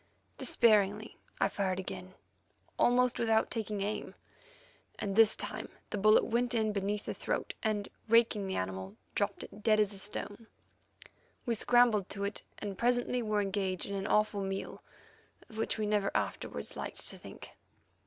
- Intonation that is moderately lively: No, narrow, 2.1 semitones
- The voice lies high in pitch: Yes, high, 210 Hz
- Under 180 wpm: Yes, average, 160 wpm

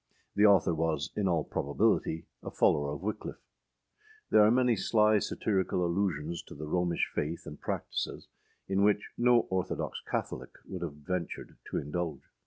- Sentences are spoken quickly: No, average, 155 wpm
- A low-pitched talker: Yes, very low, 90 Hz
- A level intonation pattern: No, average, 4.5 semitones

